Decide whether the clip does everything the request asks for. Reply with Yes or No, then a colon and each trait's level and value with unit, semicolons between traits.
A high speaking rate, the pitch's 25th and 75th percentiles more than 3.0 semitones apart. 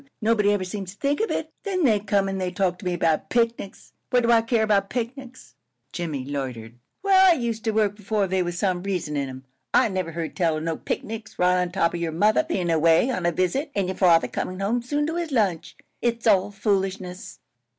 Yes: fast, 225 wpm; average, 4.6 semitones